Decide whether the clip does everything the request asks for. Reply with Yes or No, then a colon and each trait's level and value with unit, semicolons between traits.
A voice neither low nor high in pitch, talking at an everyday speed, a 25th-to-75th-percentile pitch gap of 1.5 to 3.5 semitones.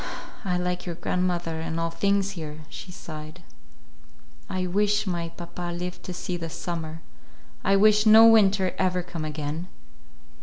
Yes: medium, 180 Hz; average, 150 wpm; narrow, 2.6 semitones